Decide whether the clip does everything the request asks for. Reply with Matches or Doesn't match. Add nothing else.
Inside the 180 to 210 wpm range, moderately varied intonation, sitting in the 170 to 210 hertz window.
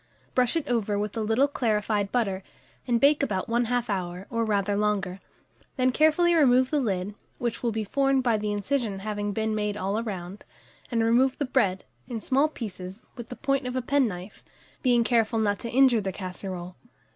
Doesn't match